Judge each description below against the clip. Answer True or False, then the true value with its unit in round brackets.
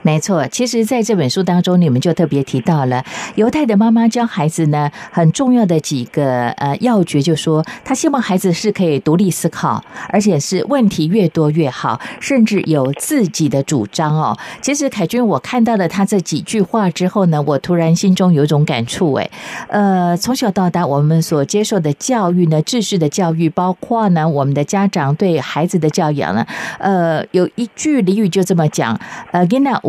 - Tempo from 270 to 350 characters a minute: True (290 characters per minute)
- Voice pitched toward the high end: False (175 Hz)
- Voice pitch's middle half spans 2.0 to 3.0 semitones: False (5.2 semitones)